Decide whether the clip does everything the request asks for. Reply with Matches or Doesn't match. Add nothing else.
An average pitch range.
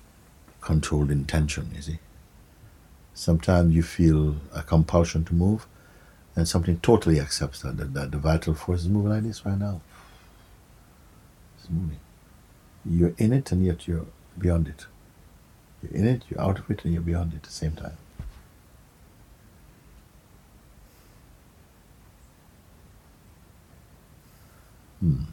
Matches